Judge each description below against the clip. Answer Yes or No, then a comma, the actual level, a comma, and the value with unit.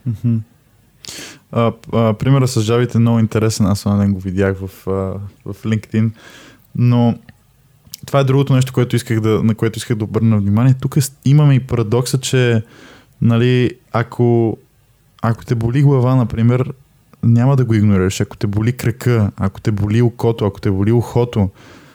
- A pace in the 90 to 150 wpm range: No, fast, 165 wpm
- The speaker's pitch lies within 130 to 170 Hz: No, low, 115 Hz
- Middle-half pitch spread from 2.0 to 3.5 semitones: Yes, narrow, 2.5 semitones